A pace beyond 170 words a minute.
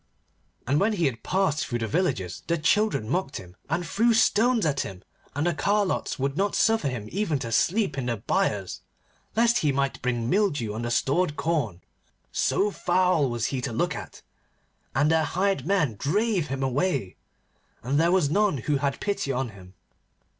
Yes: average, 180 wpm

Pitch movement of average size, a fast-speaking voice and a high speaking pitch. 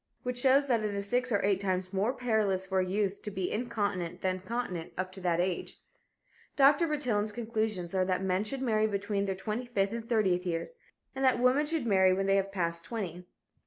Yes: average, 4.2 semitones; fast, 210 wpm; high, 200 Hz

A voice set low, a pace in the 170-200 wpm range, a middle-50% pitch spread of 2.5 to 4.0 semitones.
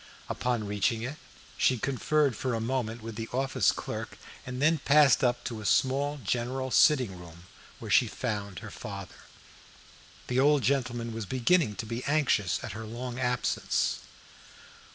No: low, 125 Hz; average, 155 wpm; average, 3.2 semitones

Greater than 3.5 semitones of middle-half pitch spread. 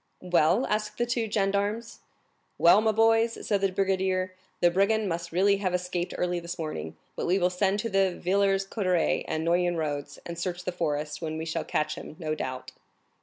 No: average, 2.9 semitones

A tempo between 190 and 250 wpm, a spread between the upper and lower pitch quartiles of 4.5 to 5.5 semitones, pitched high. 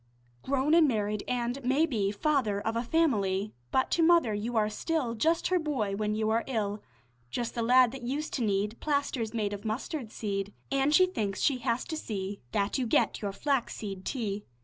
Yes: average, 195 wpm; average, 4.9 semitones; high, 230 Hz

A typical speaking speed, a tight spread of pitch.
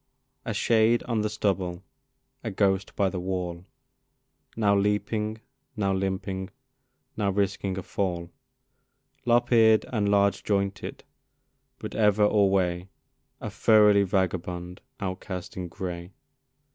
No: slow, 115 wpm; narrow, 2.3 semitones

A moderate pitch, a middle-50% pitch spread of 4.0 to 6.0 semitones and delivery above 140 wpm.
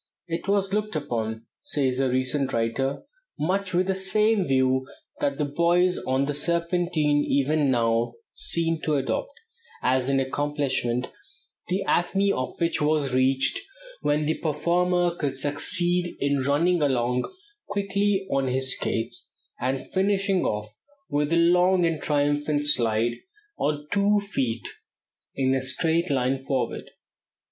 No: medium, 145 Hz; average, 5.1 semitones; slow, 135 wpm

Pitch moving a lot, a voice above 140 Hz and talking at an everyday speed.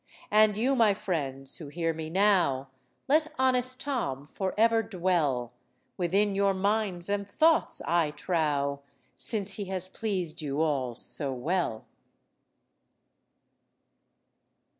No: wide, 6.0 semitones; medium, 185 Hz; slow, 120 wpm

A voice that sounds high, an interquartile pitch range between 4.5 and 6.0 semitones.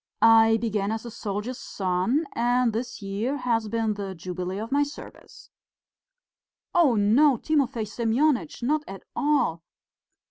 No: high, 225 Hz; average, 4.0 semitones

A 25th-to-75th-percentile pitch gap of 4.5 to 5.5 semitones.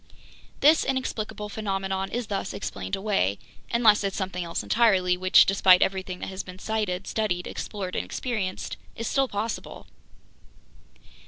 No: average, 2.8 semitones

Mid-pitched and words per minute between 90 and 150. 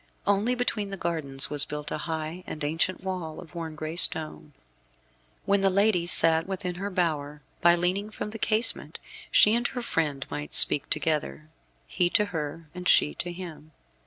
No: medium, 170 Hz; average, 175 wpm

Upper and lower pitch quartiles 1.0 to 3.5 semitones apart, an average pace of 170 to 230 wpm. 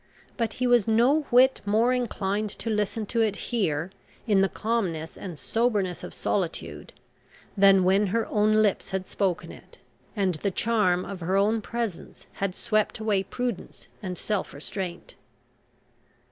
No: average, 3.1 semitones; average, 150 wpm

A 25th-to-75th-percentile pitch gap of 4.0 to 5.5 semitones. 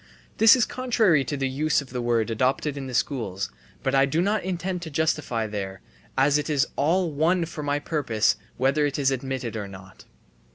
Yes: average, 4.4 semitones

